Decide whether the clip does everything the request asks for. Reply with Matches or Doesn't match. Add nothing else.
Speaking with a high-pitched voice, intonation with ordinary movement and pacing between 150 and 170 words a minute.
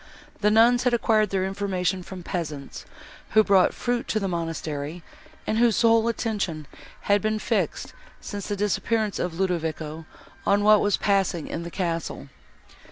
Matches